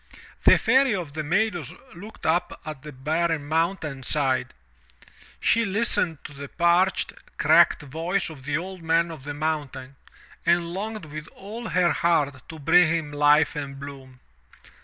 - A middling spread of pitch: Yes, average, 3.4 semitones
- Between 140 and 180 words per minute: Yes, average, 155 wpm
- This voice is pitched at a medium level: Yes, medium, 160 Hz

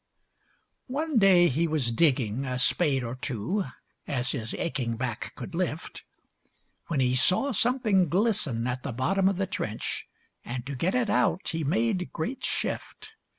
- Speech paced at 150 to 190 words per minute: Yes, average, 155 wpm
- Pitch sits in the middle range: Yes, medium, 160 Hz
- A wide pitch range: Yes, wide, 7.4 semitones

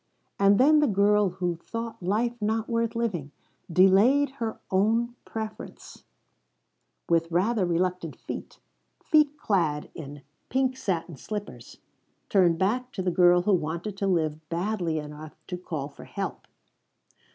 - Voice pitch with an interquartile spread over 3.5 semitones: Yes, average, 5.1 semitones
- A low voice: No, high, 195 Hz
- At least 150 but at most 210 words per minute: No, slow, 135 wpm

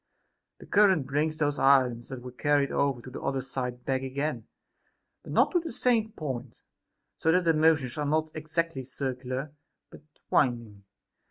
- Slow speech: No, average, 165 wpm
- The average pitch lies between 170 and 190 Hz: No, medium, 140 Hz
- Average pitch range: Yes, average, 3.5 semitones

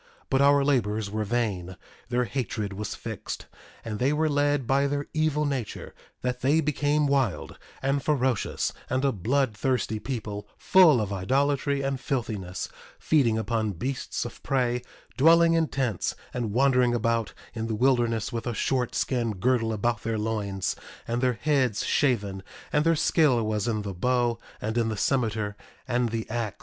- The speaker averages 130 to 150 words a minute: No, average, 160 wpm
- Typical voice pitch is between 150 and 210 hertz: No, low, 120 Hz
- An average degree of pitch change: Yes, average, 4.1 semitones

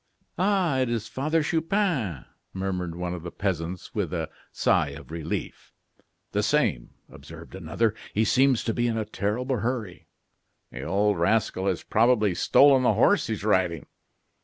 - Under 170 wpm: Yes, average, 160 wpm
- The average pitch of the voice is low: Yes, low, 105 Hz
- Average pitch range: No, wide, 6.1 semitones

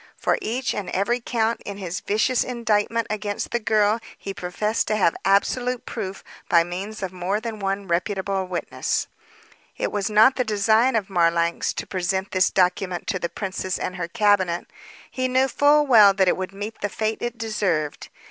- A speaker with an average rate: Yes, average, 180 wpm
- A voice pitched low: No, high, 205 Hz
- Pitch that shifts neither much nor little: Yes, average, 3.2 semitones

